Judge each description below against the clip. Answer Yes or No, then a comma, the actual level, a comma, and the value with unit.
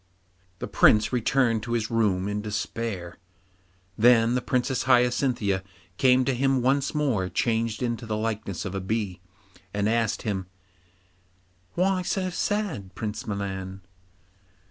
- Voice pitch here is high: No, low, 115 Hz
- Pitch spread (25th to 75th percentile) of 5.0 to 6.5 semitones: No, average, 3.7 semitones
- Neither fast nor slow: No, slow, 130 wpm